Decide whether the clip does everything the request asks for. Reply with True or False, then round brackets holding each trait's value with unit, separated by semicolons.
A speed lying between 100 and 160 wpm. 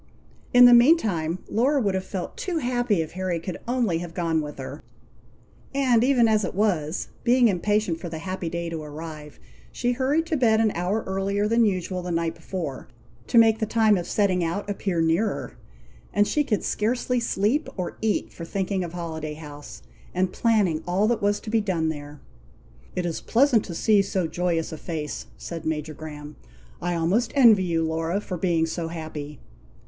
False (185 wpm)